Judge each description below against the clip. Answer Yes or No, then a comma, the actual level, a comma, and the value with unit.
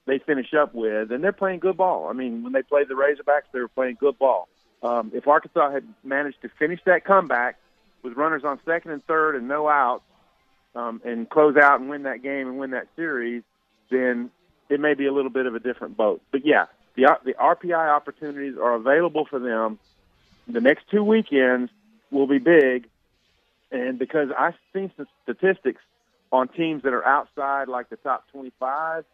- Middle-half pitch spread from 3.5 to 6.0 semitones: Yes, average, 3.9 semitones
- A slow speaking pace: No, average, 195 wpm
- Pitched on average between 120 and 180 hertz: Yes, medium, 140 Hz